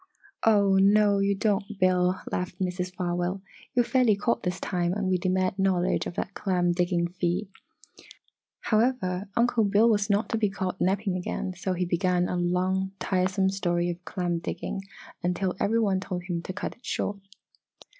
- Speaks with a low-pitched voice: No, medium, 185 Hz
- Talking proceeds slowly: No, average, 170 wpm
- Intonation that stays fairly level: Yes, narrow, 2.0 semitones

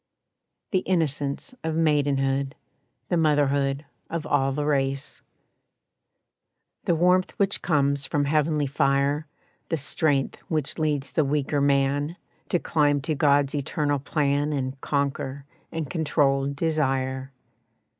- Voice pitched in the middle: Yes, medium, 145 Hz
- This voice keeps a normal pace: No, slow, 115 wpm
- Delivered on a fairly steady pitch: Yes, narrow, 2.1 semitones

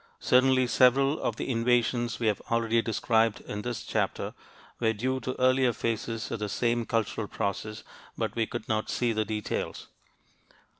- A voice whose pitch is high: No, low, 115 Hz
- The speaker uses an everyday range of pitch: No, narrow, 2.2 semitones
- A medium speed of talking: Yes, average, 160 wpm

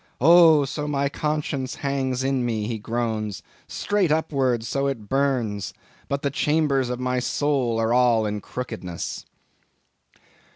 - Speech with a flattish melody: No, average, 3.4 semitones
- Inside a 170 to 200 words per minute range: No, slow, 135 wpm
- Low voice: Yes, low, 130 Hz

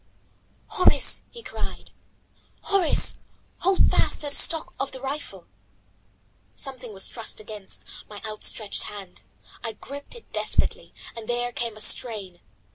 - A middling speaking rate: No, slow, 130 wpm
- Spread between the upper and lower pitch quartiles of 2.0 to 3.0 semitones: No, average, 5.0 semitones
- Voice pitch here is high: Yes, high, 240 Hz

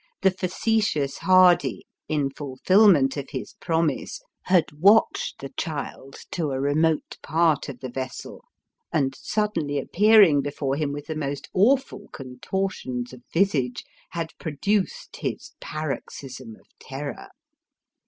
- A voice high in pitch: No, medium, 150 Hz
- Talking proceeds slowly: Yes, slow, 125 wpm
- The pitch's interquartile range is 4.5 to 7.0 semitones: Yes, average, 5.3 semitones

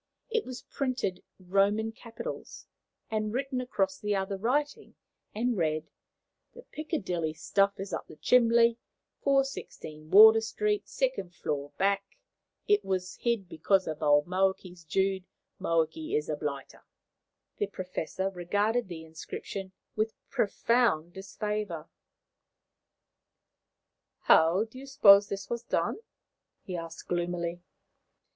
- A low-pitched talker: No, high, 200 Hz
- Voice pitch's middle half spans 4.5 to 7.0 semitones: Yes, average, 5.0 semitones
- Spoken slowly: Yes, slow, 120 wpm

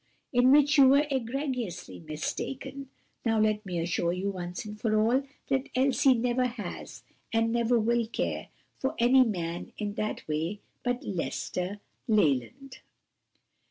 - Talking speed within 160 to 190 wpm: No, slow, 135 wpm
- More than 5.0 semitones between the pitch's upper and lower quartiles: Yes, wide, 5.4 semitones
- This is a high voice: Yes, high, 230 Hz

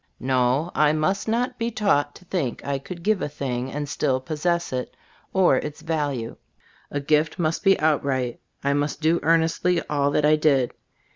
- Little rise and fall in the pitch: No, average, 3.6 semitones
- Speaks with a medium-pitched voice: Yes, medium, 150 Hz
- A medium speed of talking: Yes, average, 180 wpm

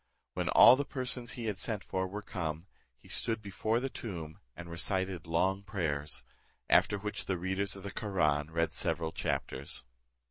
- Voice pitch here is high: No, very low, 95 Hz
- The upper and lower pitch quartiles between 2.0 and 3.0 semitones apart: No, average, 4.2 semitones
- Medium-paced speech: Yes, average, 170 wpm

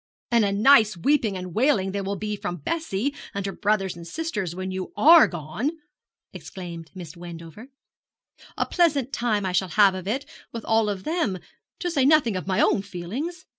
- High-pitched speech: Yes, high, 200 Hz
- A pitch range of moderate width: No, wide, 6.3 semitones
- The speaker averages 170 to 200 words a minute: Yes, average, 185 wpm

